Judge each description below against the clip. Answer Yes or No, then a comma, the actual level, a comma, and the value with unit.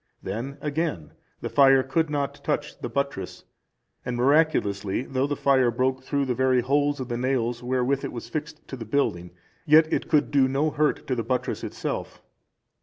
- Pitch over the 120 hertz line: Yes, low, 135 Hz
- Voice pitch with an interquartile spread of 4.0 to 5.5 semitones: No, average, 2.8 semitones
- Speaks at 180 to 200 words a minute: Yes, average, 185 wpm